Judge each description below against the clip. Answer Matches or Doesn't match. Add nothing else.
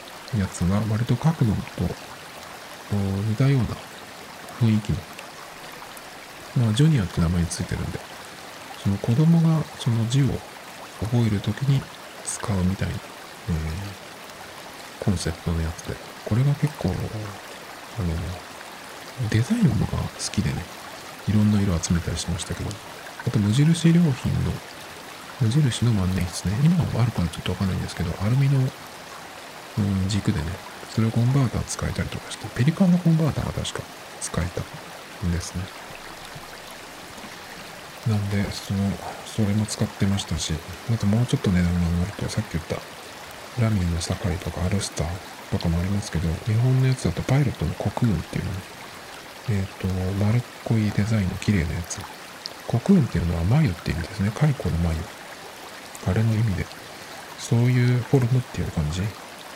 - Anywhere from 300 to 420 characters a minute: Matches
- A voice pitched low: Matches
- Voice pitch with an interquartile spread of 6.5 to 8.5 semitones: Doesn't match